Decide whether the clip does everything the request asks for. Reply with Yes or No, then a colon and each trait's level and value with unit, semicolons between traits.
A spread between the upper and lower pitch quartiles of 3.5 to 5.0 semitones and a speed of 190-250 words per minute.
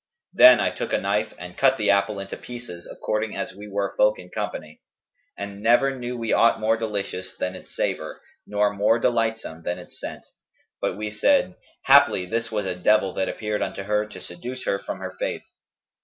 No: average, 2.8 semitones; average, 195 wpm